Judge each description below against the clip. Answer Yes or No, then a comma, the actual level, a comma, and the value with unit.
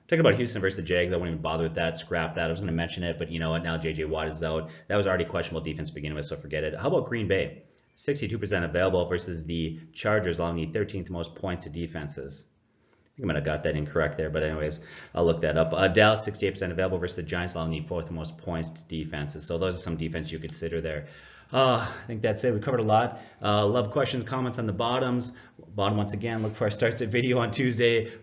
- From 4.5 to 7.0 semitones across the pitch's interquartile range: Yes, average, 5.3 semitones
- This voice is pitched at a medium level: No, very low, 90 Hz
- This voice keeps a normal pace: No, fast, 260 wpm